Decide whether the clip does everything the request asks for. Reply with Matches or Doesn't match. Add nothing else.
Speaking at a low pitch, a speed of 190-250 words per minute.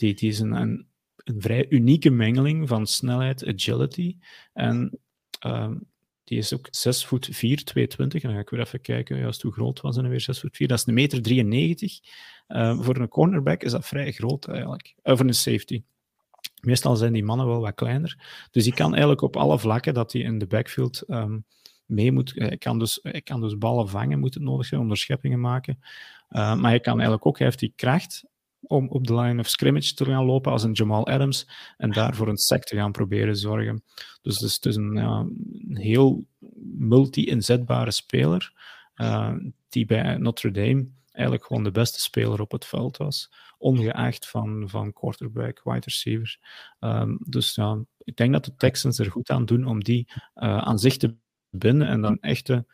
Matches